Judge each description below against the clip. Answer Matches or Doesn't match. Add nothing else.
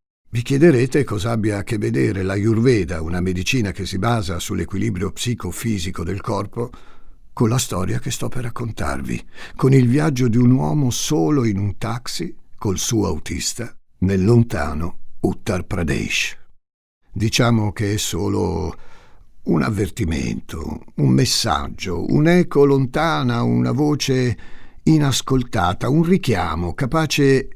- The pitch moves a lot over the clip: Matches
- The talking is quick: Doesn't match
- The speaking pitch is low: Matches